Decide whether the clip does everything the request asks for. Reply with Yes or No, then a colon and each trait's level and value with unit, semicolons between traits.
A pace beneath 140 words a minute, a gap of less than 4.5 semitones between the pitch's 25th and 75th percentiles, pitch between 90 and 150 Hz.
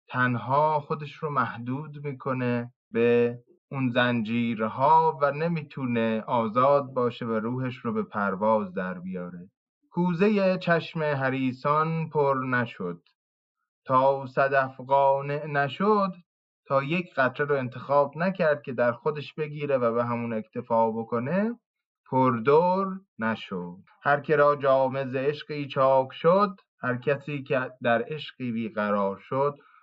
Yes: average, 120 wpm; average, 4.0 semitones; low, 135 Hz